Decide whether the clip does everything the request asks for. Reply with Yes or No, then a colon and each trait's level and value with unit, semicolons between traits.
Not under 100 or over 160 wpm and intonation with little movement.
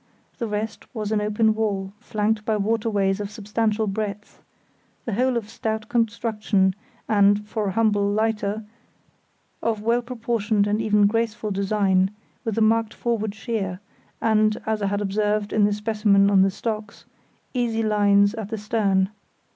Yes: average, 155 wpm; narrow, 1.6 semitones